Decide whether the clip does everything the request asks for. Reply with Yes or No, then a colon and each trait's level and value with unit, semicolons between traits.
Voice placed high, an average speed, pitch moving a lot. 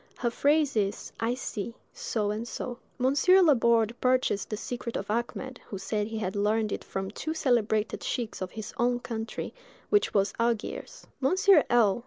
No: high, 235 Hz; average, 170 wpm; average, 3.2 semitones